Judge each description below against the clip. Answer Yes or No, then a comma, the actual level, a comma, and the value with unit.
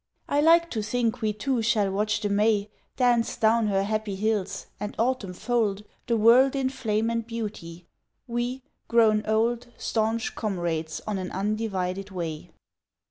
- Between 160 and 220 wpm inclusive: No, average, 150 wpm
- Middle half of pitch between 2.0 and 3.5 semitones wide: Yes, narrow, 2.6 semitones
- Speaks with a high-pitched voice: Yes, high, 215 Hz